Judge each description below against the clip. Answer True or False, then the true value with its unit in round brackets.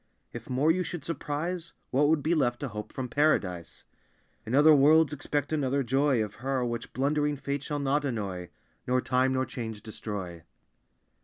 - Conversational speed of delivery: True (170 wpm)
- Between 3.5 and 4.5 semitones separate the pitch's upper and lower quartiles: True (3.8 semitones)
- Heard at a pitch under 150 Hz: True (135 Hz)